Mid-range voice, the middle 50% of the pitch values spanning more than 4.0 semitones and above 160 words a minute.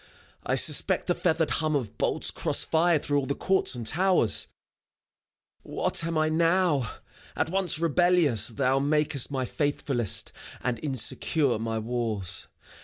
No: medium, 145 Hz; wide, 5.4 semitones; average, 140 wpm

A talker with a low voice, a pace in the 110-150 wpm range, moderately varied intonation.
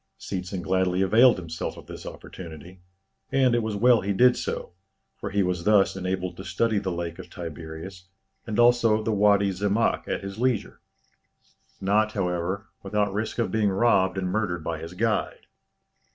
No: low, 100 Hz; average, 165 wpm; average, 3.2 semitones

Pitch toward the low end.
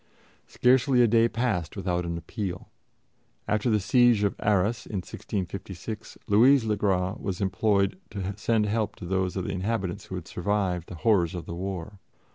Yes: low, 100 Hz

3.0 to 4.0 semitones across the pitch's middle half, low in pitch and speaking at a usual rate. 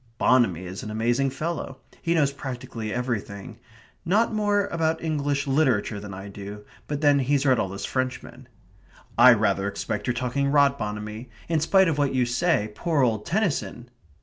No: wide, 5.4 semitones; low, 130 Hz; average, 170 wpm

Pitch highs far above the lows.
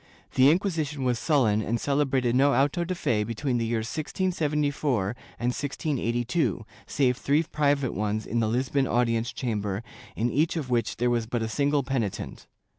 No: average, 3.9 semitones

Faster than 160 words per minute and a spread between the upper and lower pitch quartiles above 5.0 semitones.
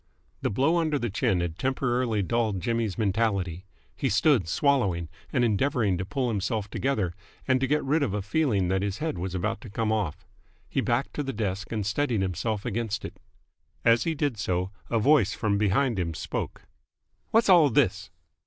Yes: average, 180 wpm; wide, 5.4 semitones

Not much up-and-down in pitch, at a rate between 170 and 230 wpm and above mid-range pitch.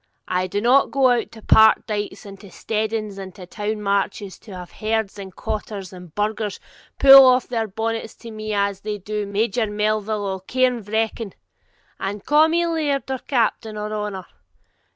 Yes: narrow, 2.1 semitones; average, 175 wpm; high, 215 Hz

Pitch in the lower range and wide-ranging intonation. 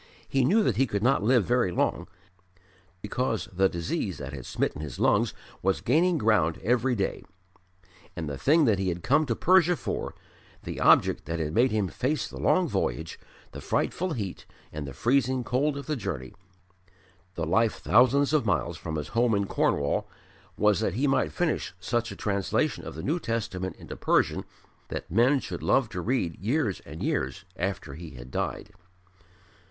Yes: low, 110 Hz; wide, 7.4 semitones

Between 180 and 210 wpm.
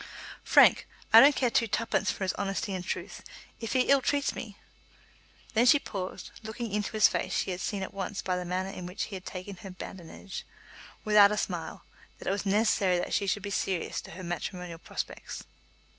Yes: fast, 205 wpm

